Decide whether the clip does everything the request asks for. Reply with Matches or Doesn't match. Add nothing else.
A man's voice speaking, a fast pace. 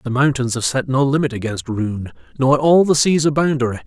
Matches